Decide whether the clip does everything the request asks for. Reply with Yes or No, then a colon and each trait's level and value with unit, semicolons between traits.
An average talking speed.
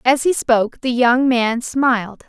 Yes: average, 185 wpm